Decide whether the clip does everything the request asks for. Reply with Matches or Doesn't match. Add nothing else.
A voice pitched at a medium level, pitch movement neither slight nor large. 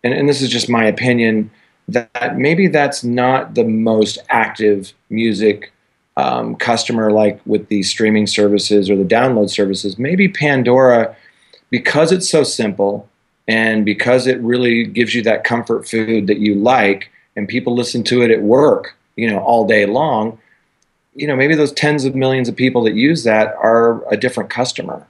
Doesn't match